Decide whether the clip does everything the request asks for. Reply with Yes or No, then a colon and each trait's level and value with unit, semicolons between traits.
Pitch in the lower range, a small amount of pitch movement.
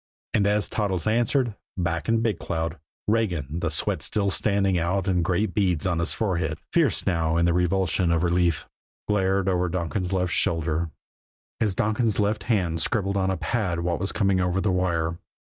No: very low, 90 Hz; average, 3.2 semitones